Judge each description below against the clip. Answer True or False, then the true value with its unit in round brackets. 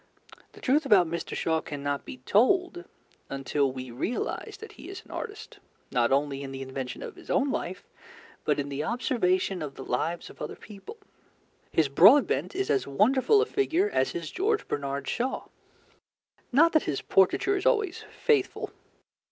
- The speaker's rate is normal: True (170 wpm)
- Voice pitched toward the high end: True (195 Hz)